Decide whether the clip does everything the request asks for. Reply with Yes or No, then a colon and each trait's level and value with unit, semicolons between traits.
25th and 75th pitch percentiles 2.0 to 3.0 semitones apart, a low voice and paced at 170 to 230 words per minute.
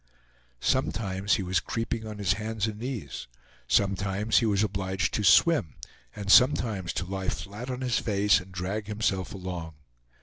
No: narrow, 2.6 semitones; low, 100 Hz; average, 160 wpm